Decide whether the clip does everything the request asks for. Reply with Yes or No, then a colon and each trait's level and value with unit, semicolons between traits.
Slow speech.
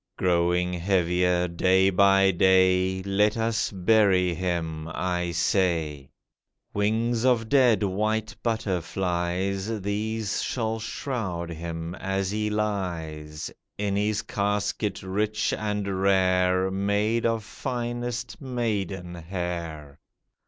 Yes: slow, 100 wpm